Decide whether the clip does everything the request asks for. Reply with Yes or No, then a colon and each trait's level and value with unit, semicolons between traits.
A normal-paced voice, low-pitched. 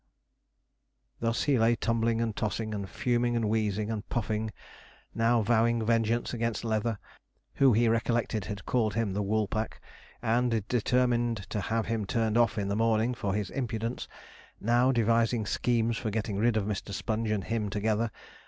Yes: average, 160 wpm; low, 115 Hz